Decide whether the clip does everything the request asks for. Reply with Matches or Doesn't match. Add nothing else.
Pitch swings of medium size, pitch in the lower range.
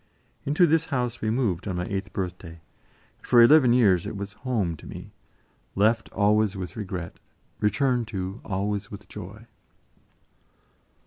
Matches